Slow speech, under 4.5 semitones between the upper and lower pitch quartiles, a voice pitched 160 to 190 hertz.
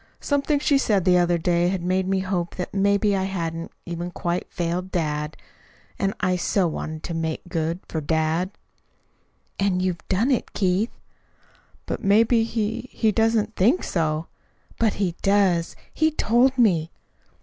No: average, 150 wpm; average, 3.8 semitones; medium, 185 Hz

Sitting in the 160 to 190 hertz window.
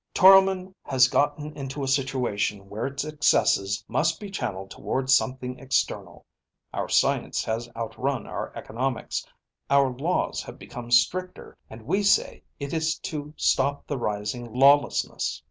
No: low, 135 Hz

